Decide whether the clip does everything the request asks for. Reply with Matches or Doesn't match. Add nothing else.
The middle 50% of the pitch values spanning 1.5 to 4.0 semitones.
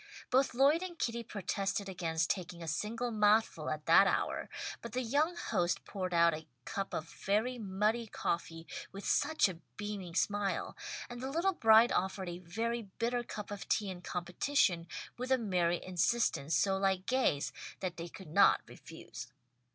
Doesn't match